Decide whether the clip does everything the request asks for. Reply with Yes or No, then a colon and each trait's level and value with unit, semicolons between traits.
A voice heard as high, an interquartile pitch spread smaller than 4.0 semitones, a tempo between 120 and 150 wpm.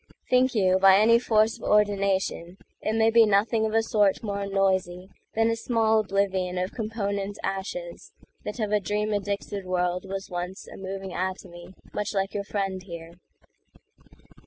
Yes: high, 200 Hz; narrow, 2.4 semitones; average, 145 wpm